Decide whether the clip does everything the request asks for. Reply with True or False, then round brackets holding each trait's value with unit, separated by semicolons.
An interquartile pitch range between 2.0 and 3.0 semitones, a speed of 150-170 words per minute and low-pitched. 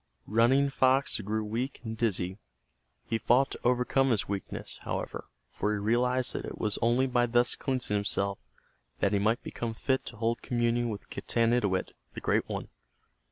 True (2.7 semitones; 165 wpm; 115 Hz)